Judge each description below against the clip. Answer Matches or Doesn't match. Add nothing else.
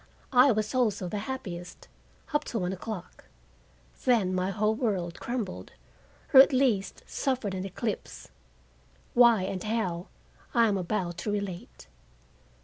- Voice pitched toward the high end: Matches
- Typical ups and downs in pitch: Matches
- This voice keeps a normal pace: Doesn't match